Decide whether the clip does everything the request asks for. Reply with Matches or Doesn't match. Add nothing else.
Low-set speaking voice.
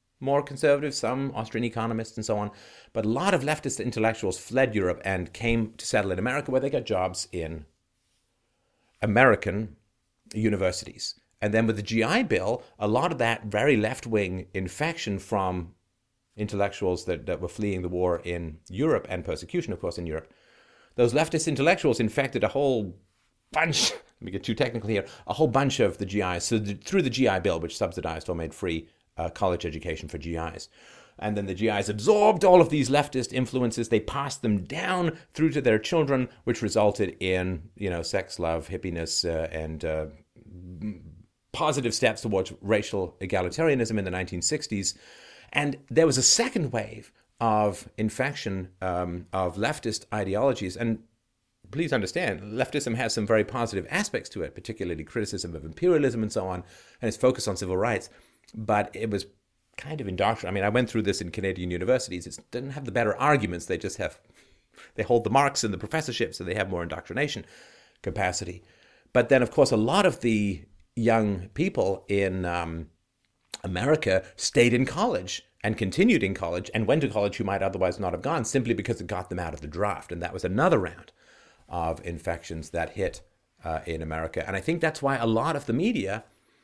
Matches